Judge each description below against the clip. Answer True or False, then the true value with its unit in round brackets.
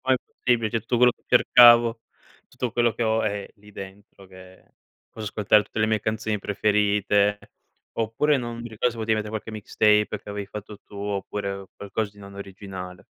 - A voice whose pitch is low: True (105 Hz)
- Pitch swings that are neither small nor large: False (2.0 semitones)